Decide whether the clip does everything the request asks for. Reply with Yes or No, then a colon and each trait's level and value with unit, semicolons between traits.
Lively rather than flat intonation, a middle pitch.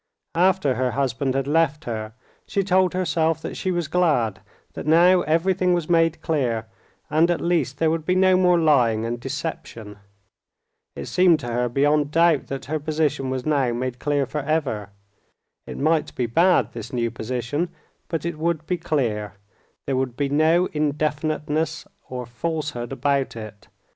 No: average, 4.7 semitones; medium, 150 Hz